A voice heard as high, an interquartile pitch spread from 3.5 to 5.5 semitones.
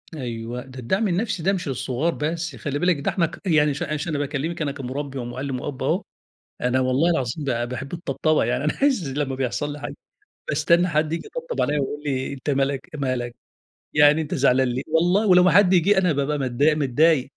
No: medium, 145 Hz; average, 4.1 semitones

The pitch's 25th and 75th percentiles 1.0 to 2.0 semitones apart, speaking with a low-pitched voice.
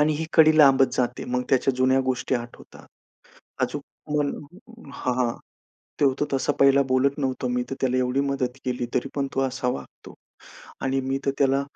Yes: narrow, 1.5 semitones; low, 130 Hz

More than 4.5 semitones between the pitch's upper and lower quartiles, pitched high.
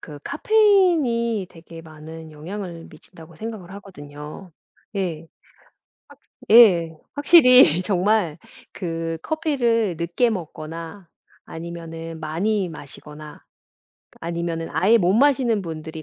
No: average, 5.3 semitones; medium, 175 Hz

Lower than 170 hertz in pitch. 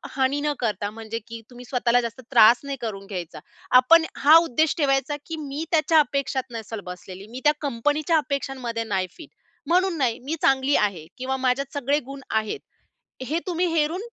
No: very high, 265 Hz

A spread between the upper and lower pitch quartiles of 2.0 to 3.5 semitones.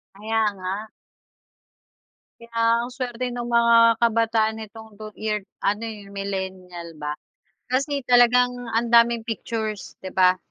Yes: average, 2.7 semitones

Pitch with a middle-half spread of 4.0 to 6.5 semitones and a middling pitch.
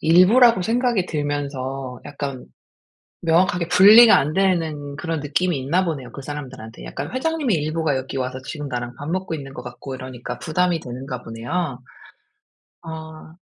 Yes: wide, 5.4 semitones; medium, 150 Hz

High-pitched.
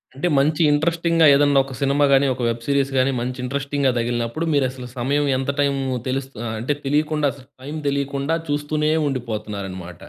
No: medium, 140 Hz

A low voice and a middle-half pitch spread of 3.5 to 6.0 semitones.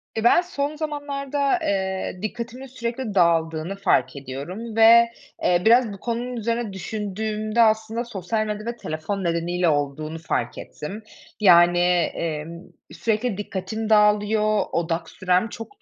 No: high, 210 Hz; average, 4.9 semitones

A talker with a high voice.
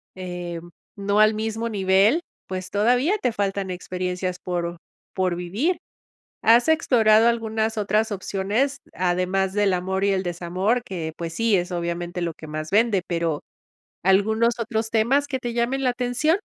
Yes: high, 200 Hz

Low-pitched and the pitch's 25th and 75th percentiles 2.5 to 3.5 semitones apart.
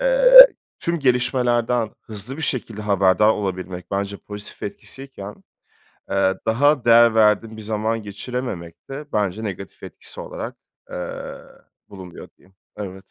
No: low, 110 Hz; average, 4.0 semitones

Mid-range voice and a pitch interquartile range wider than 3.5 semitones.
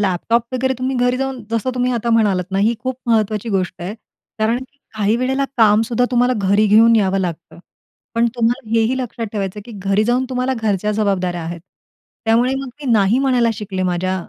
No: high, 225 Hz; average, 3.9 semitones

